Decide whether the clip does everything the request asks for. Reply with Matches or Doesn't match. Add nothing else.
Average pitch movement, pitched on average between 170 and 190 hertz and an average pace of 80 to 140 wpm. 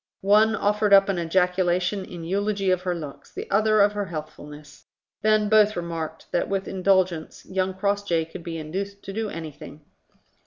Doesn't match